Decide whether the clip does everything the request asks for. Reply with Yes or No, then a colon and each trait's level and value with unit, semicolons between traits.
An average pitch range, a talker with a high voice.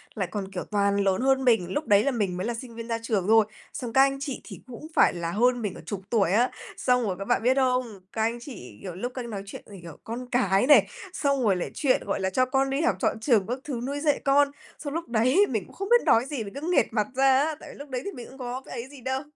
Yes: average, 4.8 semitones; high, 240 Hz